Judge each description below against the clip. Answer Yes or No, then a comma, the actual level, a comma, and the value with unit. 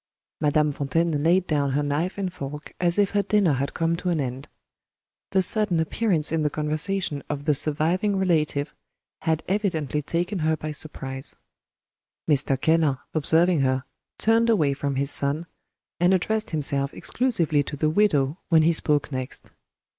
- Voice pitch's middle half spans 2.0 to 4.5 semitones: Yes, average, 3.9 semitones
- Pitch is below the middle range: No, medium, 155 Hz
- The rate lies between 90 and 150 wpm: No, average, 160 wpm